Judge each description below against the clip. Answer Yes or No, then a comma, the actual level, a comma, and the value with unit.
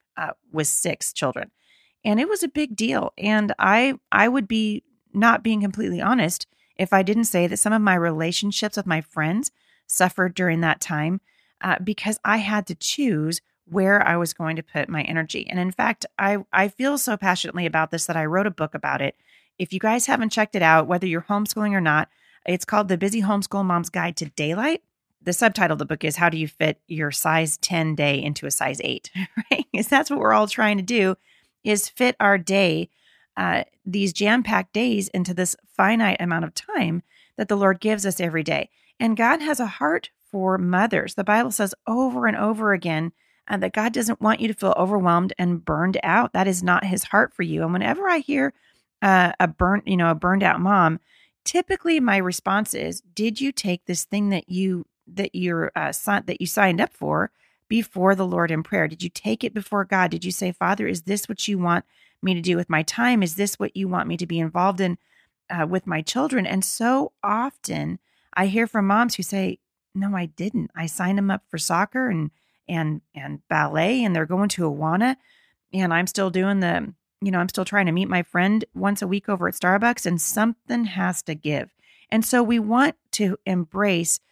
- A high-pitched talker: Yes, high, 195 Hz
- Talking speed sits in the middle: No, fast, 215 wpm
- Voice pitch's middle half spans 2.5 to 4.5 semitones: Yes, average, 3.8 semitones